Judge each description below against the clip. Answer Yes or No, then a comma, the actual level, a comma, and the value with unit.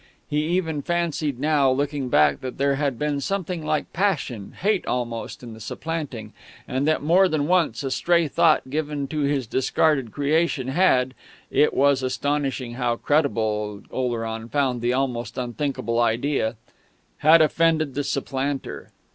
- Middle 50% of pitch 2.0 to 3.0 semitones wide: No, average, 3.8 semitones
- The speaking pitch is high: No, medium, 140 Hz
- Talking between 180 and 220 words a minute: No, average, 145 wpm